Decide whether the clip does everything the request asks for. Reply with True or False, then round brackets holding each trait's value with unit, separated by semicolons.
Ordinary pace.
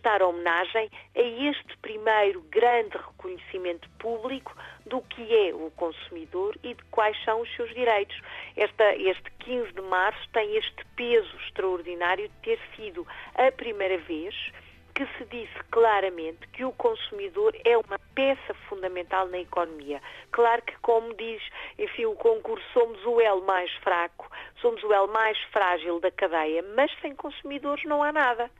True (155 wpm)